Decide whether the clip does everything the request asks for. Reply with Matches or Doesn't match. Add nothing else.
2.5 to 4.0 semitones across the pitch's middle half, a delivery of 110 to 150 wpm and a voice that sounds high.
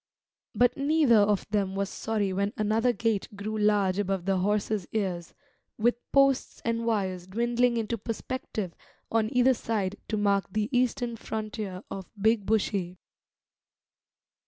Matches